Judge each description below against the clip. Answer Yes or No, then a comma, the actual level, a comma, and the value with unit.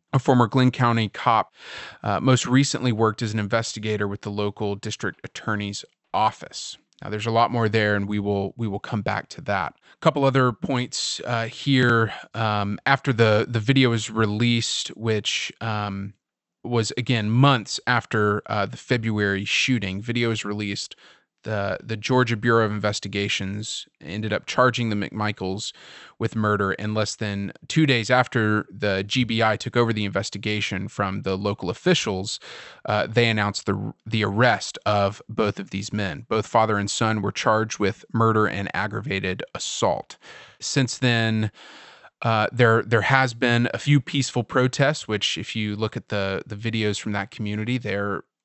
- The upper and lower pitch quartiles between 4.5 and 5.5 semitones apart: No, average, 2.7 semitones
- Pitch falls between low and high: No, low, 110 Hz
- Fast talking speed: No, average, 165 wpm